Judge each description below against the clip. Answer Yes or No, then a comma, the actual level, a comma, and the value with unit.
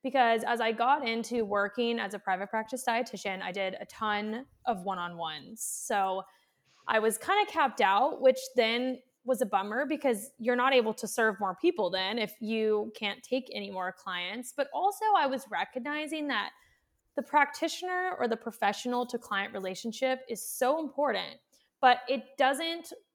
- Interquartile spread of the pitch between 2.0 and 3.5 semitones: No, average, 4.1 semitones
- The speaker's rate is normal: Yes, average, 175 wpm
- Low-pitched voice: No, high, 240 Hz